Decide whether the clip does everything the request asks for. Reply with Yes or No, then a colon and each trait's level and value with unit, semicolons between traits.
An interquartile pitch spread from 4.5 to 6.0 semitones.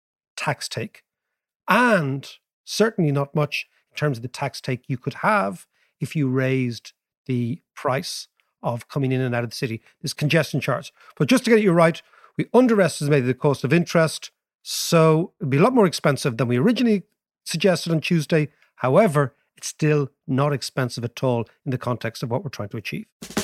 Yes: average, 5.0 semitones